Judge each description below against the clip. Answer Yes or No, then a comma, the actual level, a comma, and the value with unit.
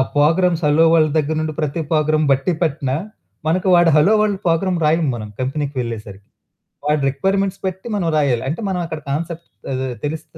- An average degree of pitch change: Yes, average, 3.2 semitones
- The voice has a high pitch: No, medium, 155 Hz